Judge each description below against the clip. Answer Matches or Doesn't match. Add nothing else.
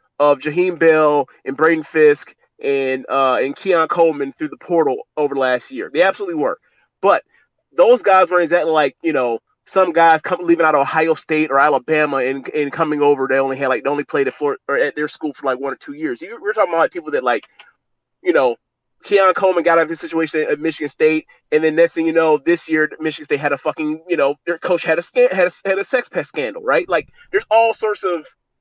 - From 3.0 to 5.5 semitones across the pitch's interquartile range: Matches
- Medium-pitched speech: Matches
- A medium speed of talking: Doesn't match